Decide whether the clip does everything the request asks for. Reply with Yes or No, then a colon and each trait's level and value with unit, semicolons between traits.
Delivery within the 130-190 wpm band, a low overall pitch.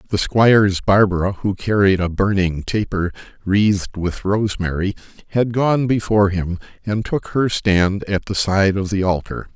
Yes: average, 155 wpm; low, 100 Hz